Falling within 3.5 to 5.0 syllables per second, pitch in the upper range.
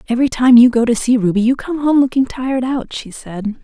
No: 5.9 syllables/s; high, 245 Hz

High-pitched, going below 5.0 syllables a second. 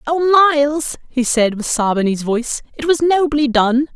Yes: very high, 270 Hz; 4.8 syllables/s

